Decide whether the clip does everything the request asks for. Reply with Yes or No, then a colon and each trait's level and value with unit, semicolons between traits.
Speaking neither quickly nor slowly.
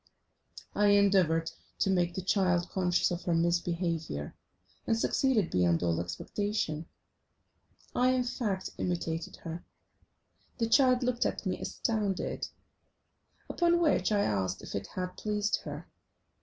No: slow, 130 wpm